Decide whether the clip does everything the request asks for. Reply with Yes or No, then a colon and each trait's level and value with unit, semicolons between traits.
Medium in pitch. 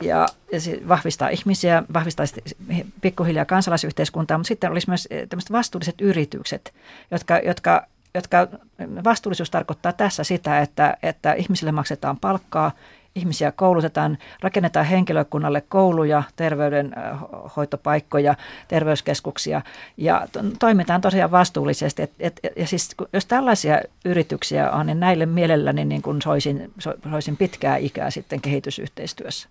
Yes: medium, 170 Hz